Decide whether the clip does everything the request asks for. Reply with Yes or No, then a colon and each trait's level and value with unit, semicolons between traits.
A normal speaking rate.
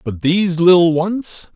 Yes: average, 155 wpm